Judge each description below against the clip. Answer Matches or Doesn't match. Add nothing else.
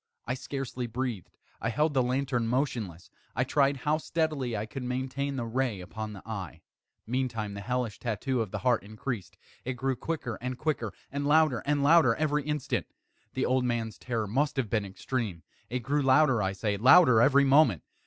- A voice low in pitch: Matches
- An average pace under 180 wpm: Doesn't match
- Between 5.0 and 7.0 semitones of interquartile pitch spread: Doesn't match